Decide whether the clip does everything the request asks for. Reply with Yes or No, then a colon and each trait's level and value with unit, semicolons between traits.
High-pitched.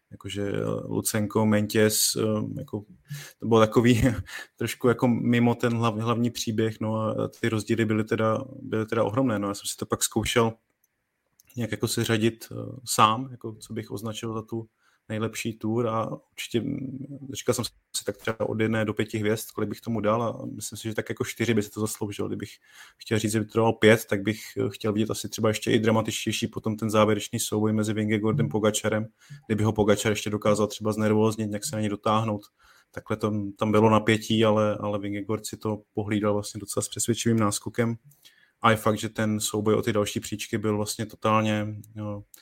No: low, 110 Hz